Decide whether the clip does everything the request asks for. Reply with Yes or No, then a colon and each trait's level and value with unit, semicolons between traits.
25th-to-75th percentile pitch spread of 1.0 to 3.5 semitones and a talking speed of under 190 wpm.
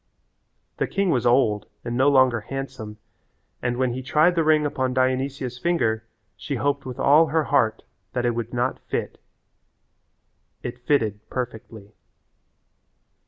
Yes: average, 3.0 semitones; average, 140 wpm